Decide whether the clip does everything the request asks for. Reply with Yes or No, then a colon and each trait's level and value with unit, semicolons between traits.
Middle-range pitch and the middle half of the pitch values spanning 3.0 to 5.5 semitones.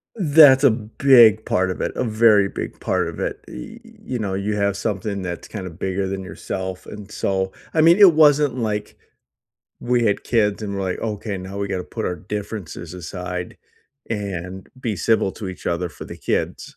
No: low, 105 Hz; average, 3.7 semitones